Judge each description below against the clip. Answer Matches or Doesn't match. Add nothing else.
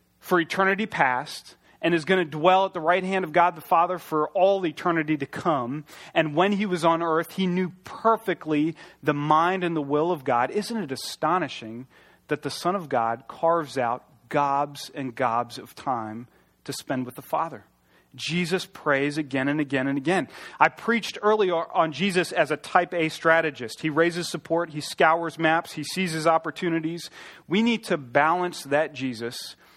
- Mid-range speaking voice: Matches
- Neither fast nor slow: Matches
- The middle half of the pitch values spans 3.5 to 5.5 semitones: Matches